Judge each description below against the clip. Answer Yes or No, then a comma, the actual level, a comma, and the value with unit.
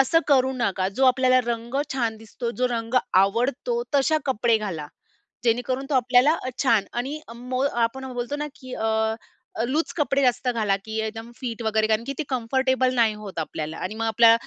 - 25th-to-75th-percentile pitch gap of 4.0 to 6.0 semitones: No, average, 3.0 semitones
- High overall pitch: Yes, high, 240 Hz